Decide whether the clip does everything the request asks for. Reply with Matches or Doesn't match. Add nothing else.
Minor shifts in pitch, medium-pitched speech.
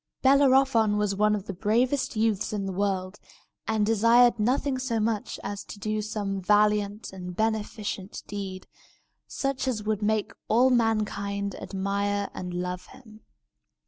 Doesn't match